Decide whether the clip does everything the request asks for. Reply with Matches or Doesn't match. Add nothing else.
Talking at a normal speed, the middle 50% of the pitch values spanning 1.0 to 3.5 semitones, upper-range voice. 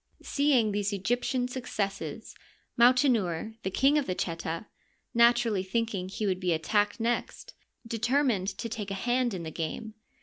Doesn't match